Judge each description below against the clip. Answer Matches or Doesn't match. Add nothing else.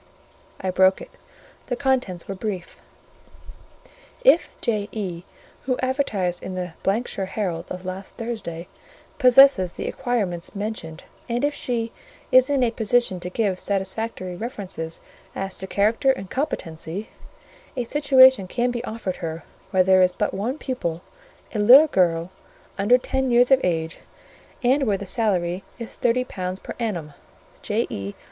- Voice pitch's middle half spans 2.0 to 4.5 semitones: Doesn't match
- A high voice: Matches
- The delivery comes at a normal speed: Matches